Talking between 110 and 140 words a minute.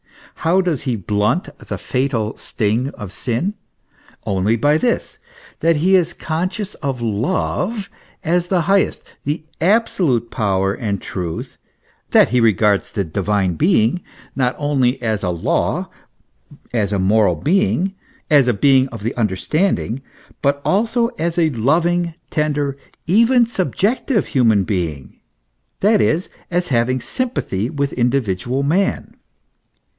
Yes: slow, 135 wpm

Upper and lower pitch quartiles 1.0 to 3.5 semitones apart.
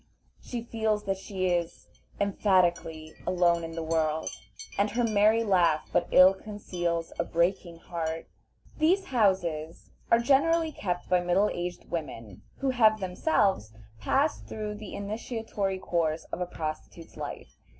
No: average, 4.2 semitones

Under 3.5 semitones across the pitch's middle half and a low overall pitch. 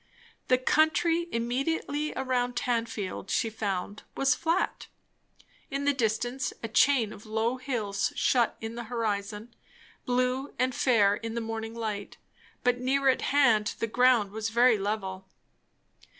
No: average, 2.9 semitones; high, 235 Hz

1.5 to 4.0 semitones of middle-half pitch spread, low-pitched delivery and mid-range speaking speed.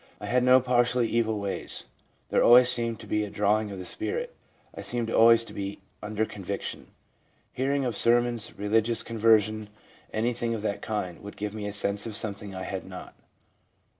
Yes: narrow, 2.6 semitones; low, 110 Hz; average, 180 wpm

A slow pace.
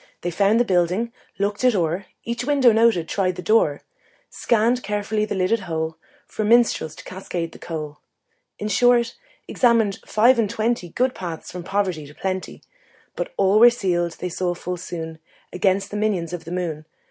No: average, 175 wpm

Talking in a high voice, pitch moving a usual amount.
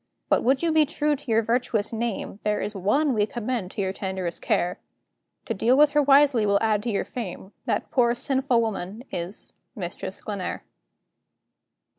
Yes: high, 225 Hz; average, 4.7 semitones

